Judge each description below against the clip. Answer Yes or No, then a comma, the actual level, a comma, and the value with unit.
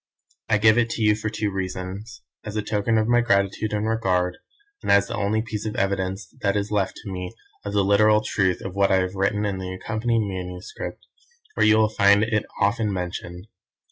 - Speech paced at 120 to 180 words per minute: No, fast, 205 wpm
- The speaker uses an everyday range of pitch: No, narrow, 2.3 semitones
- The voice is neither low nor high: No, low, 100 Hz